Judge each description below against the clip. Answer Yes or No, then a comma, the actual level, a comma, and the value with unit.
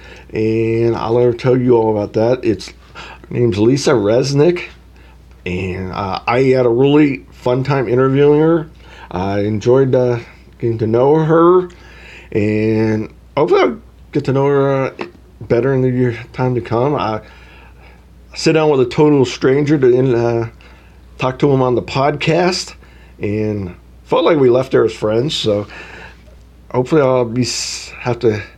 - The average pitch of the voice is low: Yes, low, 115 Hz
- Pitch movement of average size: No, wide, 6.7 semitones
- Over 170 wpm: No, average, 155 wpm